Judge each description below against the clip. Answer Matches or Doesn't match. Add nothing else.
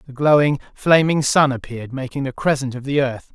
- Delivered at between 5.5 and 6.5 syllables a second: Matches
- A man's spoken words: Matches